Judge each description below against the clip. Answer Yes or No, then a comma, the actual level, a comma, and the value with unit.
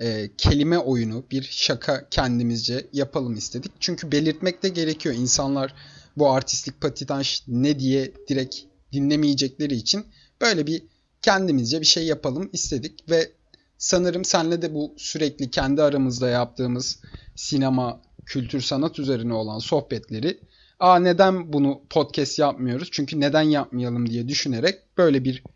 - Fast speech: No, average, 125 wpm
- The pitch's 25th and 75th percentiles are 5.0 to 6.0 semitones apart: No, average, 3.5 semitones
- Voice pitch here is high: No, medium, 140 Hz